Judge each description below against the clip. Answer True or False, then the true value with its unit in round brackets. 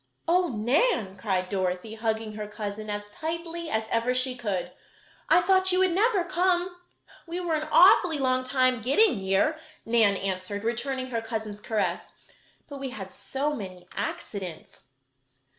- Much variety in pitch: True (7.9 semitones)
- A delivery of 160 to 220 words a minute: False (150 wpm)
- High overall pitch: True (240 Hz)